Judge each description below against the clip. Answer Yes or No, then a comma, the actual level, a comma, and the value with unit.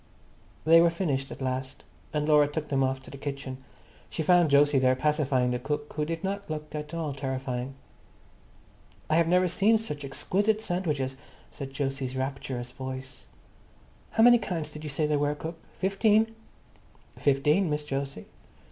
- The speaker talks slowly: No, average, 165 wpm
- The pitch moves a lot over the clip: No, average, 3.8 semitones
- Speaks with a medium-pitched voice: Yes, medium, 150 Hz